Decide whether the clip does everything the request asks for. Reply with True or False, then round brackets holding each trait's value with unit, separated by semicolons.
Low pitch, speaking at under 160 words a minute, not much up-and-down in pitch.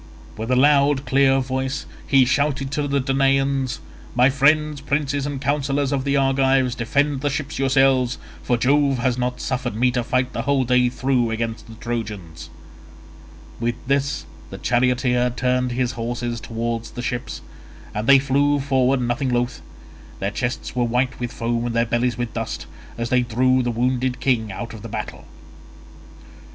False (125 Hz; 165 wpm; 2.3 semitones)